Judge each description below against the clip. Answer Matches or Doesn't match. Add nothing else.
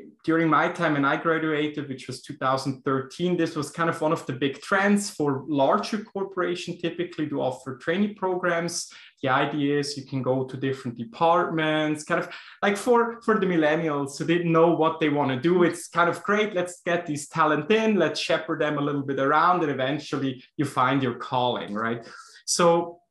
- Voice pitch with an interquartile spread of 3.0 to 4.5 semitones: Matches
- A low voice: Doesn't match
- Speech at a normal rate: Matches